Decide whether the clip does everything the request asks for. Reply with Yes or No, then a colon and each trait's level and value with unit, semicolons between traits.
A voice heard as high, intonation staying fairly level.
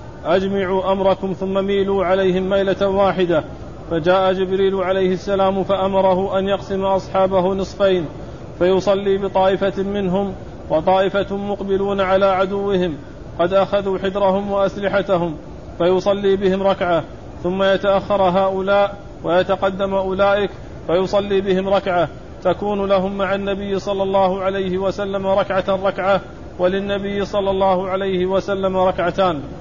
Yes: high, 195 Hz; narrow, 0.8 semitones